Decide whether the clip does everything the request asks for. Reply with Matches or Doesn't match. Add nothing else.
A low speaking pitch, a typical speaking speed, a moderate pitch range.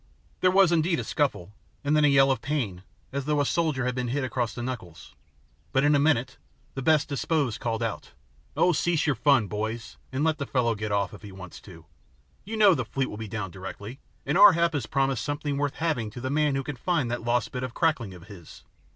Doesn't match